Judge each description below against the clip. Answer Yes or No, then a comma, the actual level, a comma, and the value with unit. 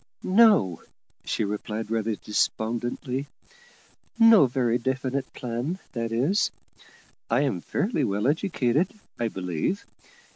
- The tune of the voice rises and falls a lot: No, average, 4.8 semitones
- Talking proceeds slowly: Yes, slow, 105 wpm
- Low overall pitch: Yes, low, 125 Hz